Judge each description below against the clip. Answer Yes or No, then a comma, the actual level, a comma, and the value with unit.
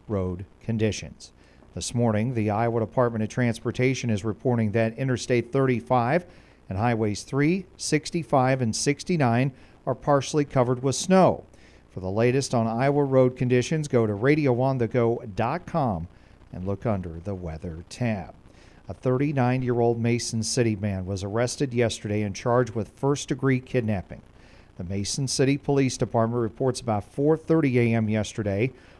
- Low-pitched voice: Yes, low, 120 Hz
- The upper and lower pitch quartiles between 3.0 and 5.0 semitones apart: Yes, average, 3.8 semitones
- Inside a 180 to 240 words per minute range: No, average, 140 wpm